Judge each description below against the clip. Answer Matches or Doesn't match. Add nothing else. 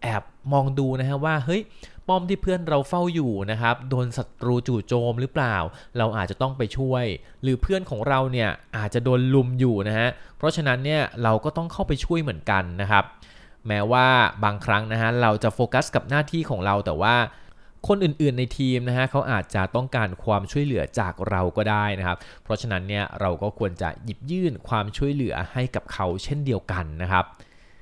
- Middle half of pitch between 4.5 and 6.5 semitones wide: Matches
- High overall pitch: Doesn't match